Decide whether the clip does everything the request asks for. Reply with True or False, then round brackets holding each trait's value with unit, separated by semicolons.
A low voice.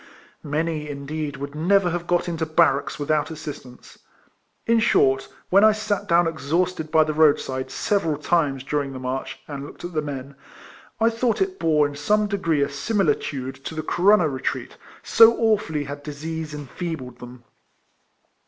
False (155 Hz)